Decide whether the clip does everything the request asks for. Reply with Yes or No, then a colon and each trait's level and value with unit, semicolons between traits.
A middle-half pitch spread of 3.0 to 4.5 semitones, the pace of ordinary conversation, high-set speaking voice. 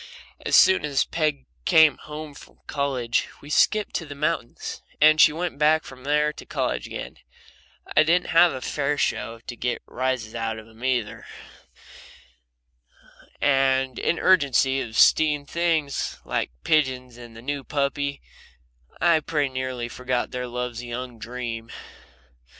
No: average, 3.5 semitones; average, 150 wpm; low, 135 Hz